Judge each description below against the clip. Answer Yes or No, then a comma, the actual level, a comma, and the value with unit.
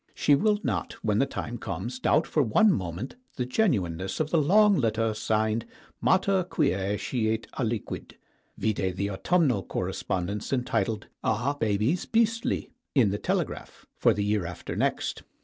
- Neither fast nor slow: Yes, average, 150 wpm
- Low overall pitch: Yes, low, 115 Hz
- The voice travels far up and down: Yes, wide, 7.4 semitones